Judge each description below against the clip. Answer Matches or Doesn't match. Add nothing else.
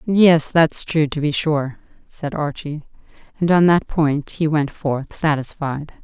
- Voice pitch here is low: Doesn't match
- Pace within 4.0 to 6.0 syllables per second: Doesn't match